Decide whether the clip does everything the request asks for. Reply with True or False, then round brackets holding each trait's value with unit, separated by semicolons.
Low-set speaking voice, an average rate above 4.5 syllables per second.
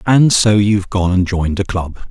True (100 Hz; 5.2 syllables/s)